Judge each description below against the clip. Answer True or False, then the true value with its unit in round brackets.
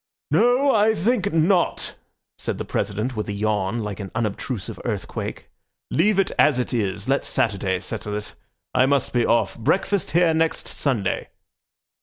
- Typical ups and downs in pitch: False (8.9 semitones)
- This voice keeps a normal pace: True (155 wpm)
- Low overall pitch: True (125 Hz)